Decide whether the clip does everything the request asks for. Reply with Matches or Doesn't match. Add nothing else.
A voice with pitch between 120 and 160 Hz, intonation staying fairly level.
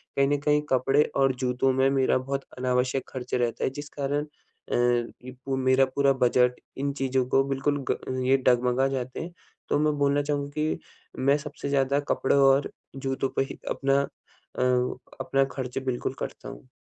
Matches